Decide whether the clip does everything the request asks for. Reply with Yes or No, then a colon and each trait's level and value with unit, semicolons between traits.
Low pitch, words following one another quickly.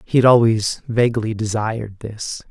No: low, 110 Hz; average, 145 wpm